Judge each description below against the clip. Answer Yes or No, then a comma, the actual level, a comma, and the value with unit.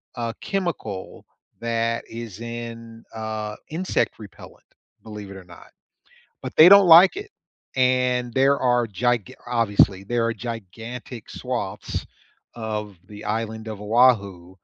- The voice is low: Yes, low, 115 Hz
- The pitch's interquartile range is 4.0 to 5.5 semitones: No, average, 2.8 semitones